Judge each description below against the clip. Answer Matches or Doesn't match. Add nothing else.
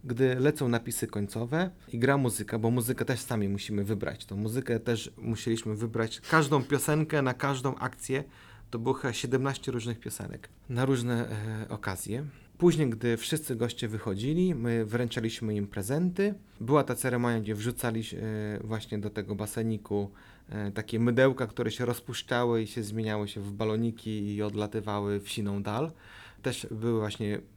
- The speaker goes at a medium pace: Matches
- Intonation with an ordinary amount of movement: Matches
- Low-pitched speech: Matches